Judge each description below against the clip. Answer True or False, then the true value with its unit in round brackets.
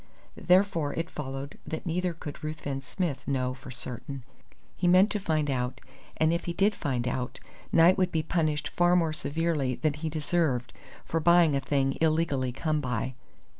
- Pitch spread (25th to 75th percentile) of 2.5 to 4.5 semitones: True (3.9 semitones)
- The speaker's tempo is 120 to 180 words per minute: True (170 wpm)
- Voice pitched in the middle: True (155 Hz)